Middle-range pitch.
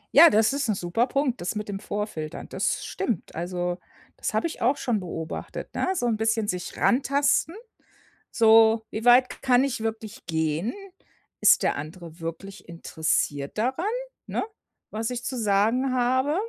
No: high, 220 Hz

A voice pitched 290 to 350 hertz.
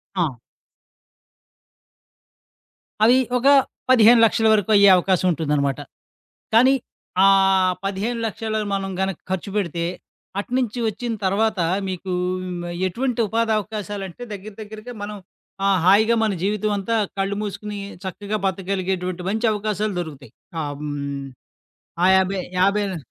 No: high, 200 Hz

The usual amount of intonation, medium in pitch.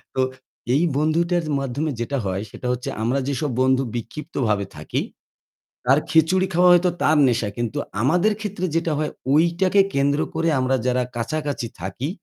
Yes: average, 5.0 semitones; medium, 145 Hz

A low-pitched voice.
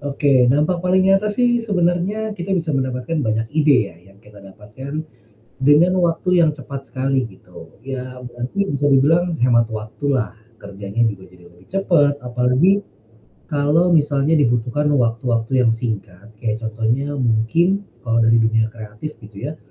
Yes: low, 130 Hz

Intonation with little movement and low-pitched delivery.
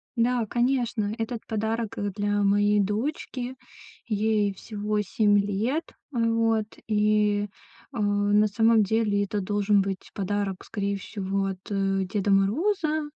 No: narrow, 2.0 semitones; high, 210 Hz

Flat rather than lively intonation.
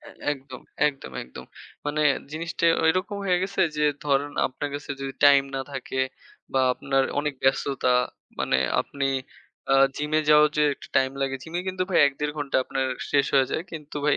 Yes: narrow, 2.3 semitones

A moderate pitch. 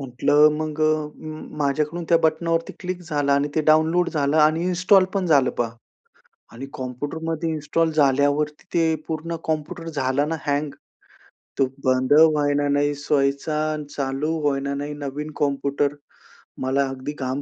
Yes: medium, 150 Hz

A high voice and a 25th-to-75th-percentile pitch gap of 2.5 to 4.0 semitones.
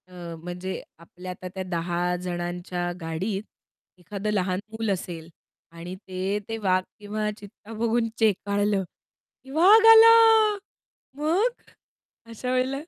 No: high, 200 Hz; average, 4.6 semitones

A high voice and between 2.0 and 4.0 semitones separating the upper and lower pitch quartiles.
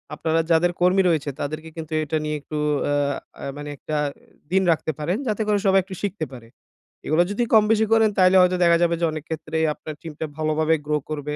No: medium, 160 Hz; average, 3.5 semitones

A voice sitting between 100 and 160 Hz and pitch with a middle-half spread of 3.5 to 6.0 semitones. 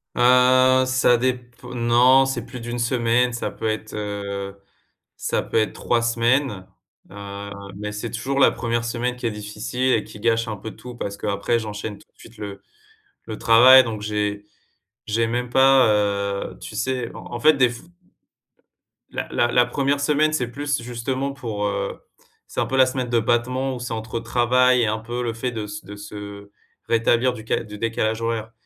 No: low, 115 Hz; average, 3.0 semitones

